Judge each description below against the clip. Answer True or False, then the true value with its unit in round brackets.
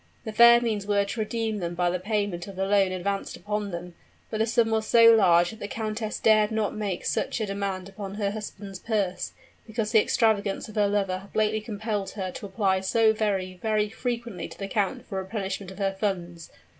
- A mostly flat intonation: True (2.2 semitones)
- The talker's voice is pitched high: True (205 Hz)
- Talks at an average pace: False (215 wpm)